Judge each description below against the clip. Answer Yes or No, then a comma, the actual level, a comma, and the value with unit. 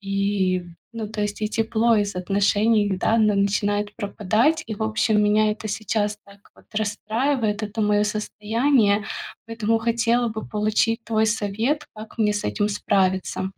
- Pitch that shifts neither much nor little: No, narrow, 1.5 semitones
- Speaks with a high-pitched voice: Yes, high, 210 Hz